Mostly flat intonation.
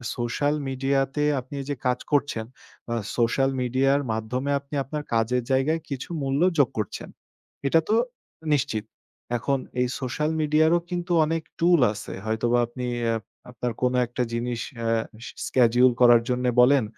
No: average, 3.1 semitones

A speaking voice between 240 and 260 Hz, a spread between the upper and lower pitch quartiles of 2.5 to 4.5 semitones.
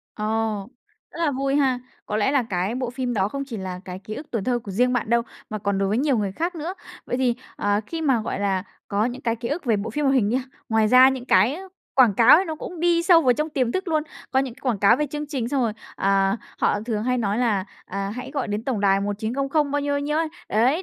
No: high, 245 Hz; average, 5.1 semitones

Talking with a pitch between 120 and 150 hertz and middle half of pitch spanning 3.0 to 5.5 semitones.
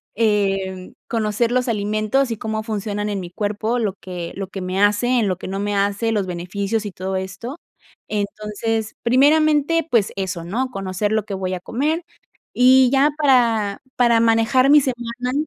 No: high, 215 Hz; average, 3.7 semitones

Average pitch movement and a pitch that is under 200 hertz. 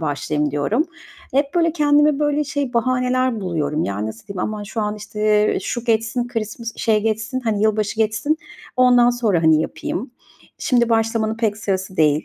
No: average, 4.4 semitones; high, 220 Hz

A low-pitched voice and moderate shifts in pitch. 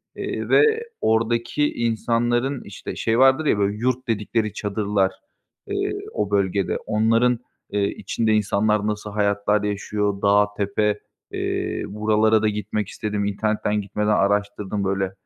No: low, 105 Hz; narrow, 1.7 semitones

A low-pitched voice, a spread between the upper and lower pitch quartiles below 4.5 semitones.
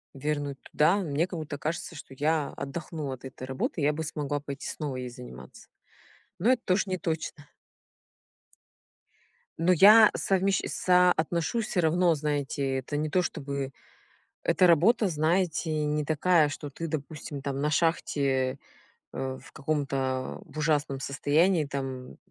No: medium, 150 Hz; average, 3.4 semitones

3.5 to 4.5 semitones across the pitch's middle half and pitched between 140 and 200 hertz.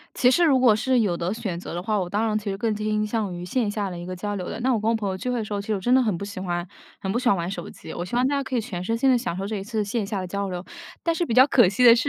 No: average, 4.0 semitones; high, 210 Hz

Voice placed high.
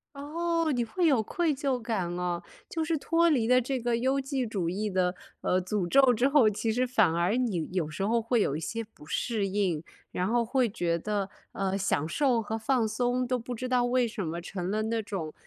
Yes: high, 225 Hz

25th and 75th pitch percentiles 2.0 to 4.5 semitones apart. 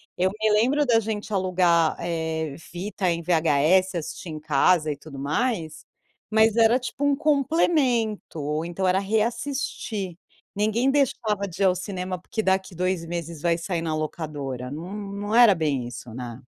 No: average, 5.3 semitones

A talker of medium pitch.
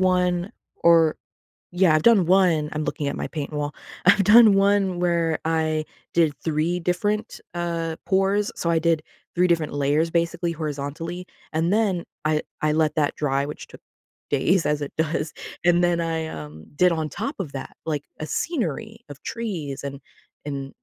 Yes: medium, 165 Hz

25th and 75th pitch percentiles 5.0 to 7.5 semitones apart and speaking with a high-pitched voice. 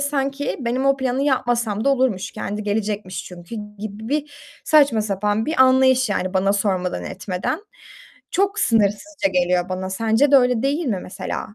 Yes: wide, 5.4 semitones; high, 225 Hz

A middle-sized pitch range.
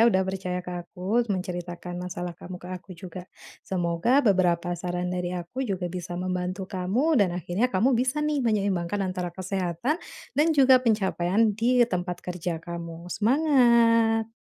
Yes: average, 4.5 semitones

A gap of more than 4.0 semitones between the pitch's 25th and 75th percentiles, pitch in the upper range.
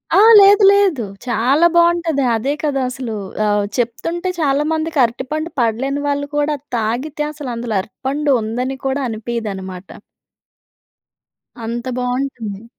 Yes: average, 4.6 semitones; very high, 265 Hz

